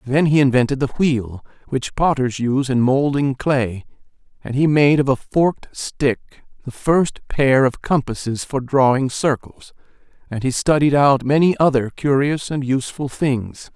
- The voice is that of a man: Yes, male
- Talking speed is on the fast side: No, average, 155 wpm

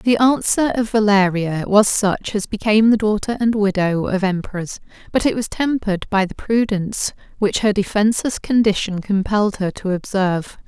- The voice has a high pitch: Yes, high, 205 Hz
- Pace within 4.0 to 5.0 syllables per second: No, 5.2 syllables/s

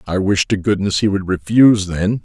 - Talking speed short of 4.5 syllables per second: No, 5.3 syllables/s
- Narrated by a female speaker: No, male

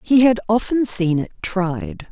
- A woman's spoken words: Yes, female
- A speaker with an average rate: Yes, average, 170 wpm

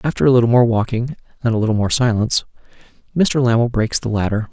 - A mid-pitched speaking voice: No, low, 120 Hz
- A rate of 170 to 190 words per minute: No, average, 200 wpm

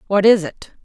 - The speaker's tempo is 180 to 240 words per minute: Yes, fast, 215 wpm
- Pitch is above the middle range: Yes, high, 200 Hz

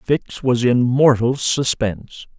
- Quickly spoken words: No, slow, 125 wpm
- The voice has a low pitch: Yes, low, 125 Hz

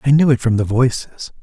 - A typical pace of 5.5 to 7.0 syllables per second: Yes, 5.7 syllables/s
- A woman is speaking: No, male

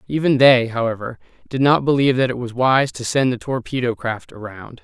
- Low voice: Yes, low, 125 Hz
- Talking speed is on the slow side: No, average, 200 wpm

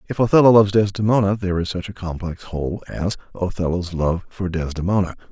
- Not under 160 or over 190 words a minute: Yes, average, 170 wpm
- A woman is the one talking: No, male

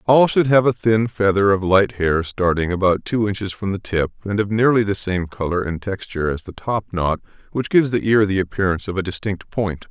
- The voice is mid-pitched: No, low, 100 Hz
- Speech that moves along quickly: Yes, fast, 225 wpm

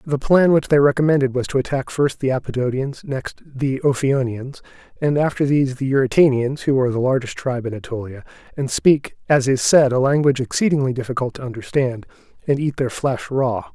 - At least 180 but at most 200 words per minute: Yes, average, 185 wpm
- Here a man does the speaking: Yes, male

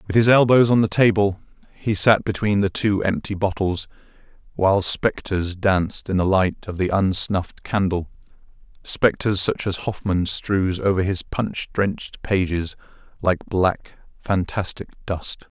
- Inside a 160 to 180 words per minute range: No, average, 140 wpm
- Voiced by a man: Yes, male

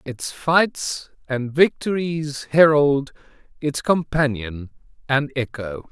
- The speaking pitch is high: No, medium, 140 Hz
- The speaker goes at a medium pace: No, slow, 90 wpm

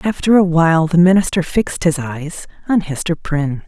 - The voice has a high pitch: No, medium, 170 Hz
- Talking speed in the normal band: Yes, average, 165 wpm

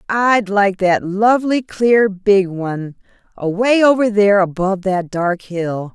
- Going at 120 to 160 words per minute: Yes, average, 140 wpm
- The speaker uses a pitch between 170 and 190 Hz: No, high, 200 Hz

